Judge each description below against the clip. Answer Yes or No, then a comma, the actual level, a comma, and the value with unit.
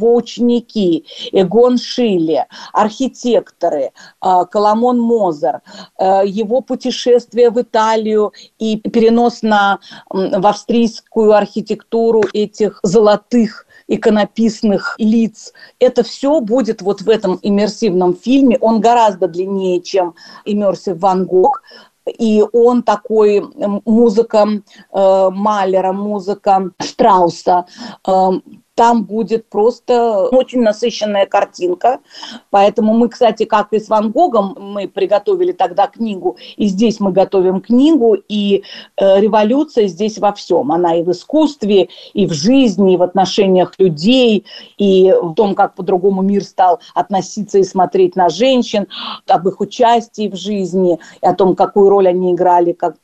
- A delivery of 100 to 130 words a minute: Yes, average, 120 wpm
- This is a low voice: No, high, 210 Hz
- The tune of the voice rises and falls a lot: No, average, 3.3 semitones